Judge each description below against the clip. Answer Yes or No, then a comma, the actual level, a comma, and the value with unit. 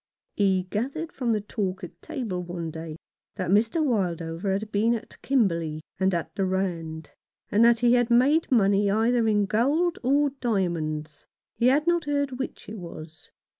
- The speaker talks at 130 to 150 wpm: No, average, 170 wpm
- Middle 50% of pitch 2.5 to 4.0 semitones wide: No, wide, 5.6 semitones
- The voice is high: Yes, high, 205 Hz